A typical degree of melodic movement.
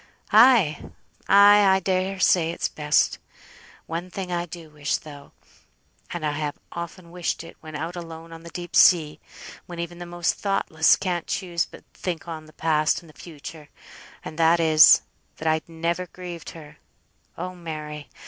No: narrow, 2.2 semitones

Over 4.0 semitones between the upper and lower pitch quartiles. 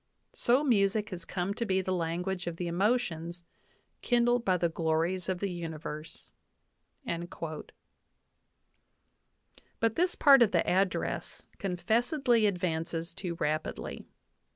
Yes: average, 4.6 semitones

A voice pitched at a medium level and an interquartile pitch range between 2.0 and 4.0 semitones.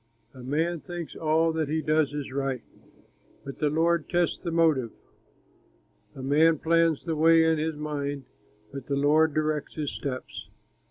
Yes: medium, 155 Hz; narrow, 2.5 semitones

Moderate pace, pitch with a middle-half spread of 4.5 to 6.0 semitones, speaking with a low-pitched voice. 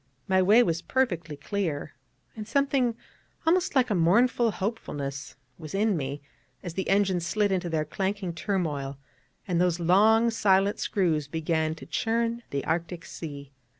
No: average, 150 wpm; average, 5.2 semitones; medium, 185 Hz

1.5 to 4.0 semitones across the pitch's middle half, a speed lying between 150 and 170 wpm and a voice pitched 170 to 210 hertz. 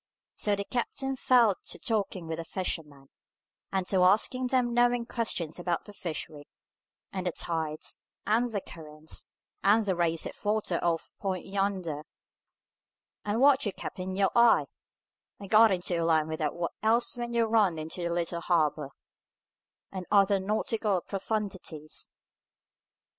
No: average, 4.6 semitones; average, 155 wpm; high, 190 Hz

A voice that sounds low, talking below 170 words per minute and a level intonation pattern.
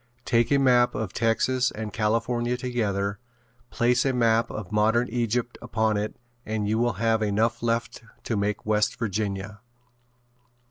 Yes: low, 115 Hz; average, 145 wpm; narrow, 2.1 semitones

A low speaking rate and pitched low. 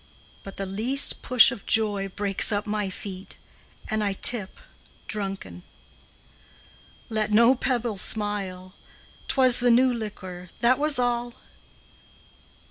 No: slow, 125 wpm; high, 215 Hz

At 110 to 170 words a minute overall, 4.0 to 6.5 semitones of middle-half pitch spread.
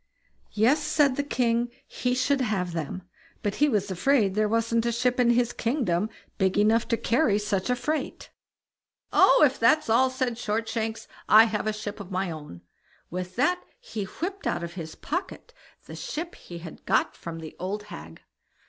No: average, 180 wpm; average, 4.8 semitones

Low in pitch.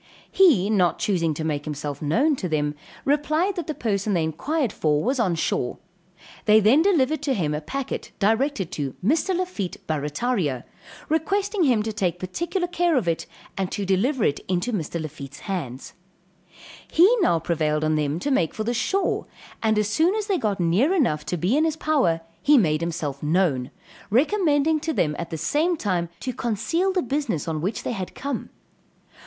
No: high, 210 Hz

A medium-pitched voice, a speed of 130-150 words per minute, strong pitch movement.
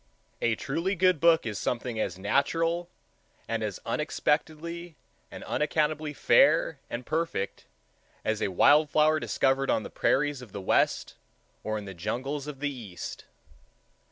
Yes: medium, 145 Hz; average, 145 wpm; wide, 5.7 semitones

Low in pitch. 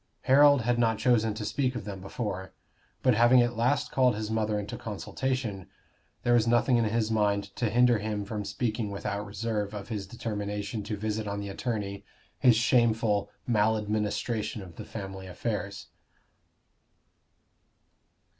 Yes: low, 110 Hz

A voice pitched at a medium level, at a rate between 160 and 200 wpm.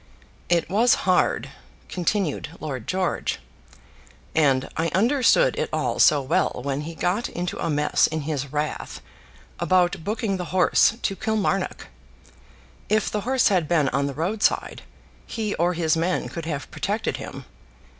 No: medium, 175 Hz; average, 145 wpm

